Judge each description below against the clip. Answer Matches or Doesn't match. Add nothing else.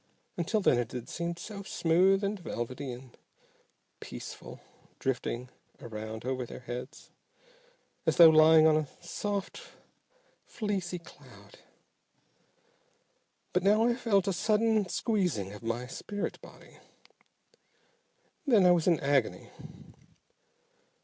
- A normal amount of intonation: Doesn't match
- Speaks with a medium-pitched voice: Matches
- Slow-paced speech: Matches